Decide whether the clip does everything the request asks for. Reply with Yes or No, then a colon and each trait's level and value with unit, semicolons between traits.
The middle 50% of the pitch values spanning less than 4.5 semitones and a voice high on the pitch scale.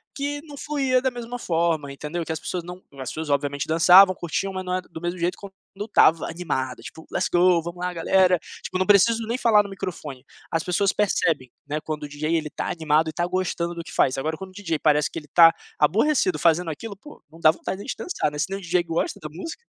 No: average, 3.9 semitones; medium, 175 Hz